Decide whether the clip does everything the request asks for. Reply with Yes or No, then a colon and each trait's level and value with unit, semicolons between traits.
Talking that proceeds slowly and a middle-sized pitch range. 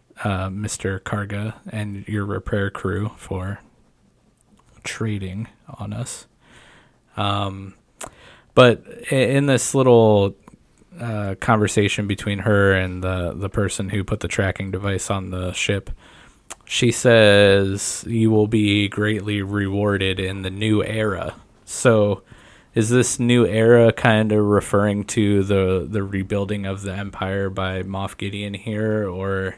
No: slow, 130 wpm; narrow, 2.0 semitones